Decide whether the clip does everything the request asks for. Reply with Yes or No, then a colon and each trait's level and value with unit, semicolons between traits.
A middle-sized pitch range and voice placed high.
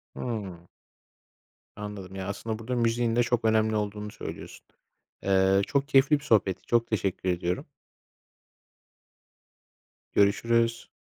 No: average, 3.2 semitones; low, 110 Hz